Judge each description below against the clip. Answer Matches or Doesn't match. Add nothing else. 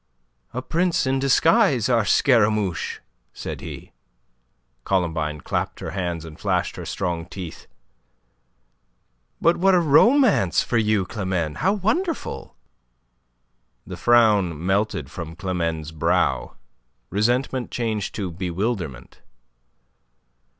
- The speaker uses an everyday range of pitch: Doesn't match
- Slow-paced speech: Matches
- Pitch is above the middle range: Doesn't match